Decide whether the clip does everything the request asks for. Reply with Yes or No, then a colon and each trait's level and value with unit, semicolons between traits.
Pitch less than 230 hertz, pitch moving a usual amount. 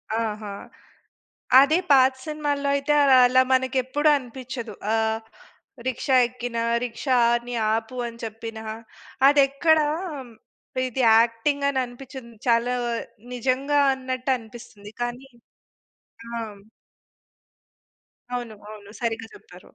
No: very high, 250 Hz; average, 3.0 semitones